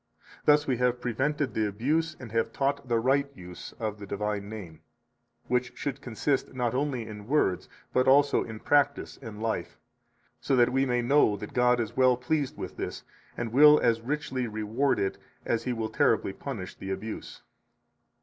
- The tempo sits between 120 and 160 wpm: No, average, 180 wpm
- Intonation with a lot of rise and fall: No, average, 4.0 semitones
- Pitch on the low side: Yes, low, 125 Hz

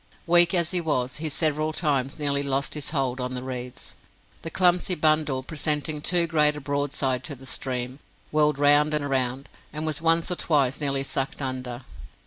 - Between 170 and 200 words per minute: Yes, average, 180 wpm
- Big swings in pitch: No, average, 2.8 semitones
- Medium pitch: Yes, medium, 145 Hz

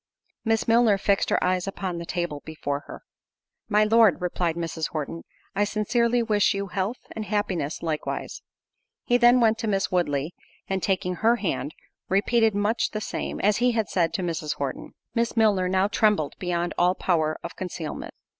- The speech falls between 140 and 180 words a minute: Yes, average, 175 wpm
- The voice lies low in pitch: No, high, 195 Hz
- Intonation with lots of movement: No, average, 4.2 semitones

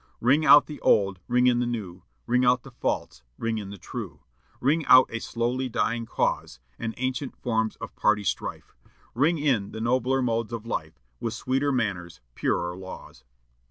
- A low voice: Yes, low, 120 Hz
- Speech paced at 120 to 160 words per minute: No, average, 175 wpm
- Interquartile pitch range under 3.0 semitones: No, average, 3.3 semitones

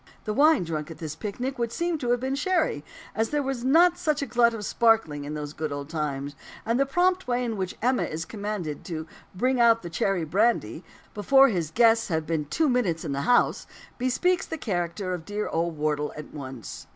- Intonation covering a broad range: Yes, wide, 8.3 semitones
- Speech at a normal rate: No, fast, 215 wpm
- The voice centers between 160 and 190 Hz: No, high, 210 Hz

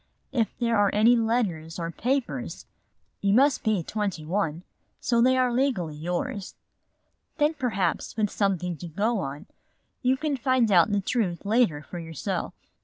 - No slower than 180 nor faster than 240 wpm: No, average, 155 wpm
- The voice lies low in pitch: No, high, 210 Hz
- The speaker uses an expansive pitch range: Yes, wide, 5.9 semitones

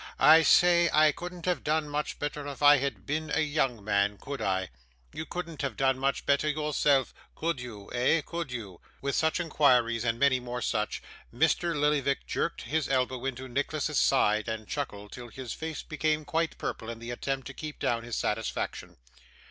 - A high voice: No, medium, 140 Hz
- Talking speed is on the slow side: No, average, 185 wpm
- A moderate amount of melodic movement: Yes, average, 4.2 semitones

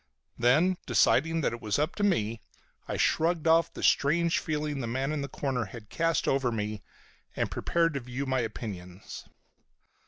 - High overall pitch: No, low, 135 Hz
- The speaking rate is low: No, average, 165 wpm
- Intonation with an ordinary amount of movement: No, wide, 5.8 semitones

